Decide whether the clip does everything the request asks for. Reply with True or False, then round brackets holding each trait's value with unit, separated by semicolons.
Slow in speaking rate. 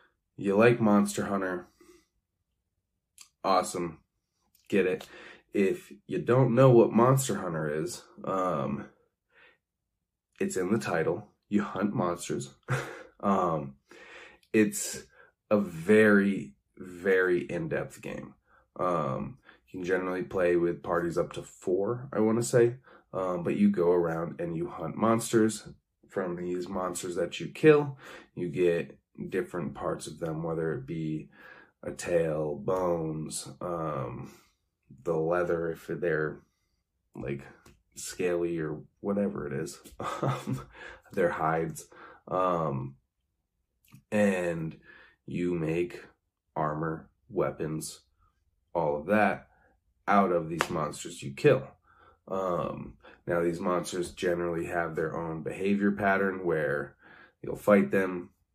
True (115 wpm)